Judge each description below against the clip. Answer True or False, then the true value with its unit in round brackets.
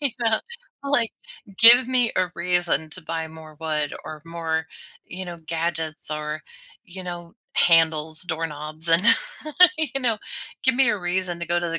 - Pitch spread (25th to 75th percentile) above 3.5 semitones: False (2.8 semitones)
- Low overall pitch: False (170 Hz)